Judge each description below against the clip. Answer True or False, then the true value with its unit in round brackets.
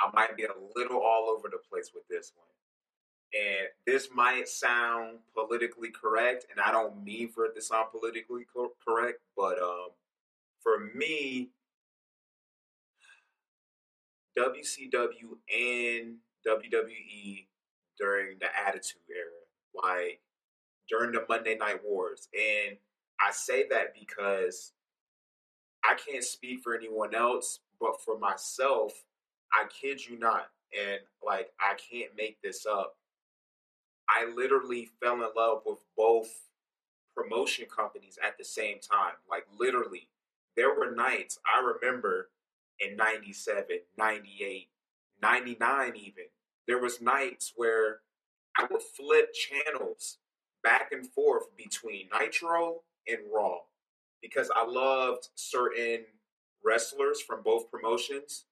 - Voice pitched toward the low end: False (170 Hz)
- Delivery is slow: True (120 wpm)